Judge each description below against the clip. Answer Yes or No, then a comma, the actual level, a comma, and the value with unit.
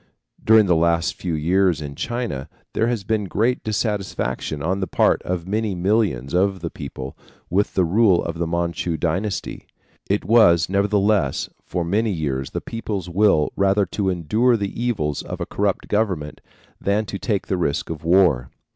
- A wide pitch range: No, average, 4.0 semitones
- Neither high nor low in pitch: No, very low, 95 Hz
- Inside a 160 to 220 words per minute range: Yes, average, 170 wpm